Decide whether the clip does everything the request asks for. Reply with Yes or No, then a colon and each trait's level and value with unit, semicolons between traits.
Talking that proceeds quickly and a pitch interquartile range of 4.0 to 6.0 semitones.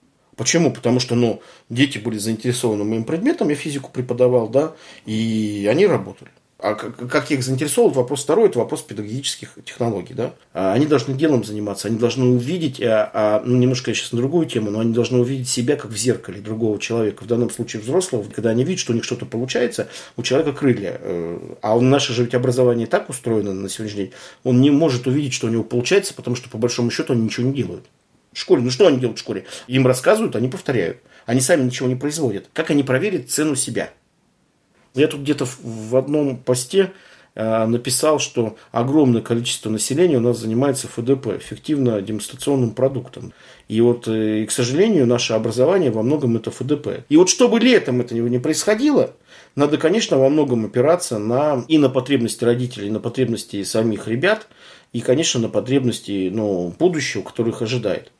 No: fast, 190 wpm; average, 3.5 semitones